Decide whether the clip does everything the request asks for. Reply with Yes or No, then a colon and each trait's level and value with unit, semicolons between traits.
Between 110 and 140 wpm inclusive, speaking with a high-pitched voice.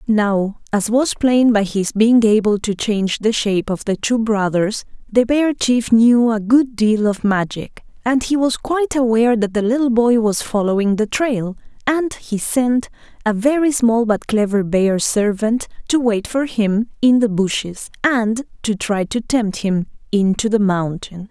No: average, 180 wpm; high, 225 Hz